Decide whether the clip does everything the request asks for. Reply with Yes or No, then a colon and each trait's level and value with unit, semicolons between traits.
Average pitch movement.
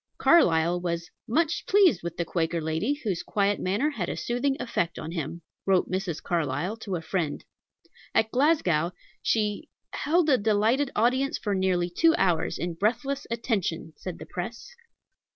No: wide, 6.1 semitones